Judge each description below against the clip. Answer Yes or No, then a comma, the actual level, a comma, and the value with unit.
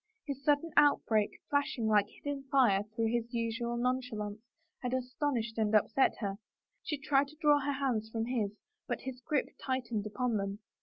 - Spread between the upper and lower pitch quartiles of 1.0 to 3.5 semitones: No, average, 4.0 semitones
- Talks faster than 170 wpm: No, average, 165 wpm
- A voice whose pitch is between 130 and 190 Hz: No, high, 245 Hz